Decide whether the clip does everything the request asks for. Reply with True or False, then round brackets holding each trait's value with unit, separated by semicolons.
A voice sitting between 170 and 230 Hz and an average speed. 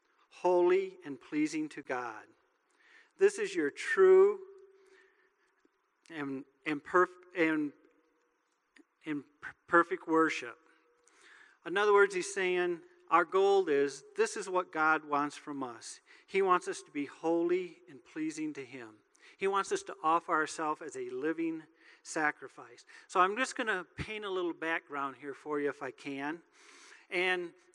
True (185 Hz; 145 wpm)